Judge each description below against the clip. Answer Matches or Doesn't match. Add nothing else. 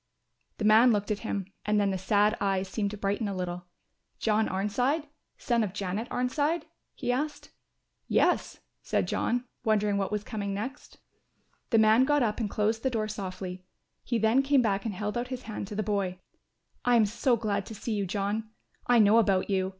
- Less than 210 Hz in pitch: Doesn't match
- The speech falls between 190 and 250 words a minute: Matches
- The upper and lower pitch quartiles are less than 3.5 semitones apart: Matches